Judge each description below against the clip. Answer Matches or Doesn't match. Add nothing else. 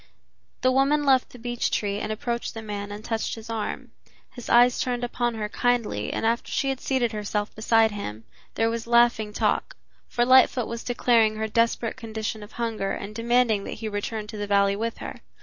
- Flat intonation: Matches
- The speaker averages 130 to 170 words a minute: Doesn't match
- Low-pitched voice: Doesn't match